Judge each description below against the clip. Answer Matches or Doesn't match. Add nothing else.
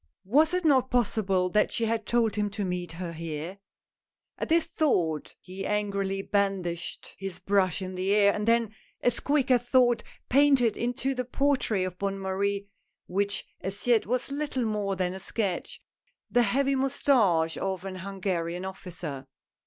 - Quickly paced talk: Doesn't match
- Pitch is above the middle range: Matches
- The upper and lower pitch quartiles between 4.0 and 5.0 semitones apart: Matches